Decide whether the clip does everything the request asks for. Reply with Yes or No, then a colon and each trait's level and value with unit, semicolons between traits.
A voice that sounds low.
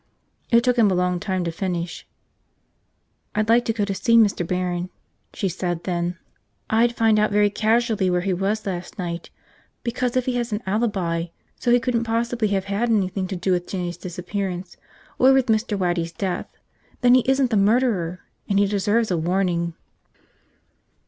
No: high, 200 Hz